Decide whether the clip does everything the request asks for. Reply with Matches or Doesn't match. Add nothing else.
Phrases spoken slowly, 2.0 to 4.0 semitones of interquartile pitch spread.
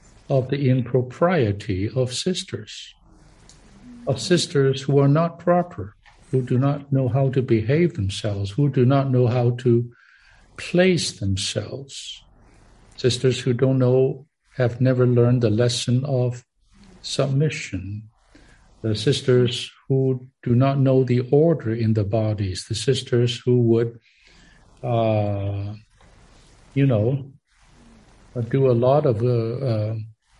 Matches